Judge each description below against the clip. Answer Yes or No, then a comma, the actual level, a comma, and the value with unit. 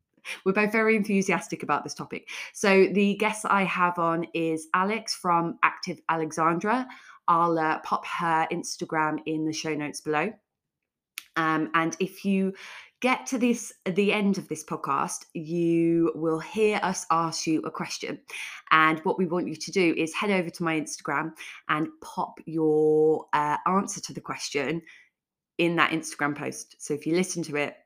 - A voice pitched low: No, medium, 165 Hz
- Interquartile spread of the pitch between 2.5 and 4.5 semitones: Yes, average, 3.4 semitones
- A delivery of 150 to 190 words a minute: Yes, average, 170 wpm